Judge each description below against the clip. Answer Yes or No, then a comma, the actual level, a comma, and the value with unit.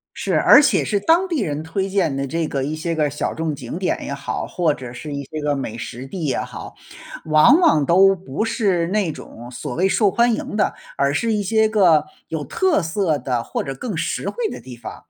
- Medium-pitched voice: Yes, medium, 160 Hz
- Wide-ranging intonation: Yes, wide, 6.2 semitones